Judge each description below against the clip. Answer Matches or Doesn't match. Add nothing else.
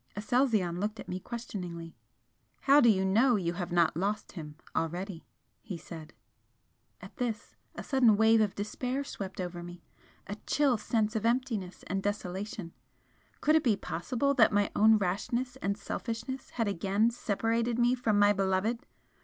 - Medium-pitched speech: Doesn't match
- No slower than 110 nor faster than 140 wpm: Doesn't match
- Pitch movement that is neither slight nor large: Matches